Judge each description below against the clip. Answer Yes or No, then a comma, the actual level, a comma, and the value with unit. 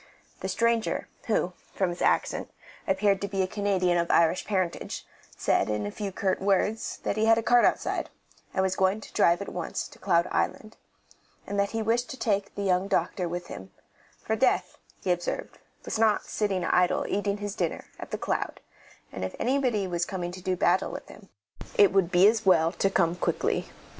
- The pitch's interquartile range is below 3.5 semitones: Yes, average, 2.7 semitones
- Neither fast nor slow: Yes, average, 195 wpm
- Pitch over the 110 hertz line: Yes, high, 190 Hz